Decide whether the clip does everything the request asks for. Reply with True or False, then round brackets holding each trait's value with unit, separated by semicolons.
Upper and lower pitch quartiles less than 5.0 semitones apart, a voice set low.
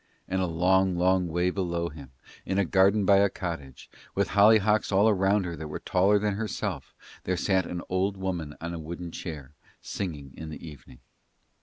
True (2.8 semitones; 90 Hz)